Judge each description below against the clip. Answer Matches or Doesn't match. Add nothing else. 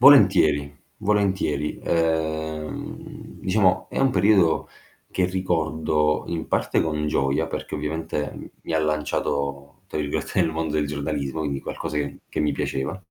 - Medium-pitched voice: Doesn't match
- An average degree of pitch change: Matches